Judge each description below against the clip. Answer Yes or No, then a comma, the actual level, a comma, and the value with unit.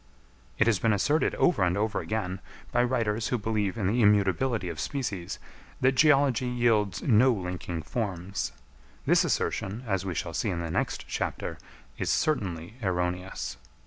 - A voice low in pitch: Yes, low, 105 Hz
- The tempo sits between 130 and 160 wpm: Yes, average, 155 wpm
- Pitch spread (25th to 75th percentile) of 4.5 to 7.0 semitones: Yes, average, 4.9 semitones